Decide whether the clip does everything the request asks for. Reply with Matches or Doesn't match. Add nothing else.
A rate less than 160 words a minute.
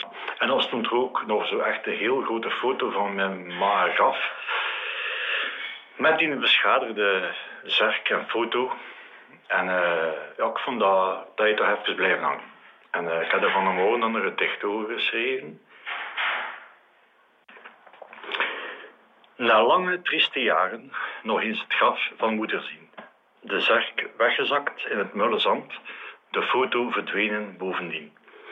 Matches